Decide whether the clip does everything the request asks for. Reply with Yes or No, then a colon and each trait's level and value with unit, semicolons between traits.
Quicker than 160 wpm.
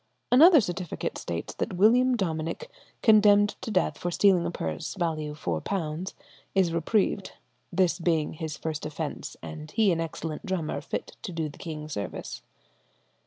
No: average, 150 wpm